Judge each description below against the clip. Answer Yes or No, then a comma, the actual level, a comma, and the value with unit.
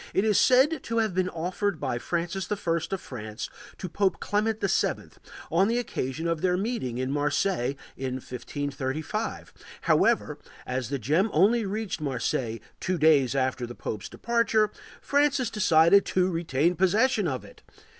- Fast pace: No, average, 155 wpm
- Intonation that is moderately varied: No, wide, 7.5 semitones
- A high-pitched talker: No, medium, 175 Hz